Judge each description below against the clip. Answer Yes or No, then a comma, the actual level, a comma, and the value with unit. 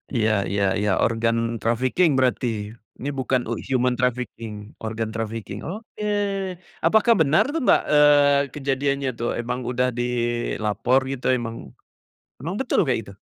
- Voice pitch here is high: No, low, 125 Hz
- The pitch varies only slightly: No, average, 3.4 semitones